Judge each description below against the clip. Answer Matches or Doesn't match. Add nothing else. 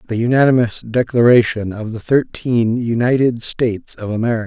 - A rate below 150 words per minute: Matches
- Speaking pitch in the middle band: Doesn't match